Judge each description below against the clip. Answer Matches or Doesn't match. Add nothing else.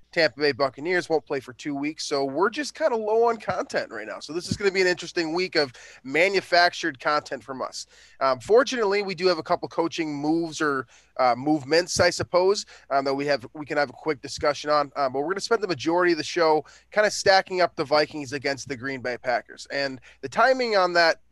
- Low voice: Doesn't match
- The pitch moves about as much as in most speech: Matches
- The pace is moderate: Doesn't match